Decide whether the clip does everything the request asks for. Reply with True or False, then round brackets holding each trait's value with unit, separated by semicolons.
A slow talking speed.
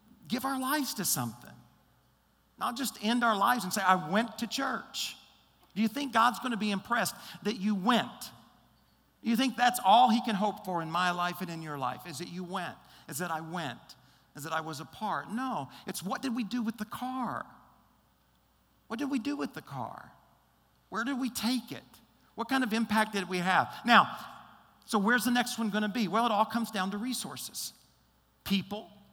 False (205 wpm)